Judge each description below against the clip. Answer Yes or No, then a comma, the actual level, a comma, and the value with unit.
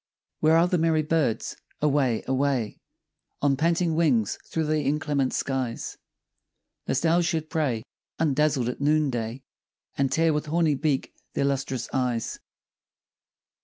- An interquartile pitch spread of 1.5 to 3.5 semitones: Yes, average, 3.2 semitones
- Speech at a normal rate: No, slow, 130 wpm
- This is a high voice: No, medium, 145 Hz